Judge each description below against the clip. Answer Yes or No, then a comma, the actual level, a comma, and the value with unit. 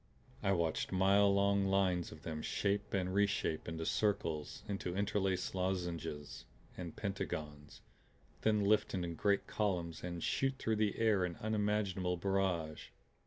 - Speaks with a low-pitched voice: Yes, very low, 95 Hz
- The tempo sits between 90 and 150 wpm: Yes, slow, 135 wpm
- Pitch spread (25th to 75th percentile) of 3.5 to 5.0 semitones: No, average, 2.9 semitones